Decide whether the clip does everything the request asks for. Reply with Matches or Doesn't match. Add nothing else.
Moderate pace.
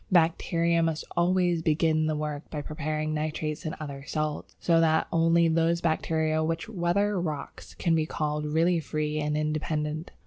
Matches